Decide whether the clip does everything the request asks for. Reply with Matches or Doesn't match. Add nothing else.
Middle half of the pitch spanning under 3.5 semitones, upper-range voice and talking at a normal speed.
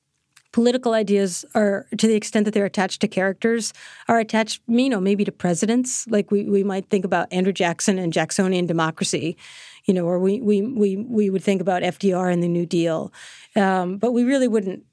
Matches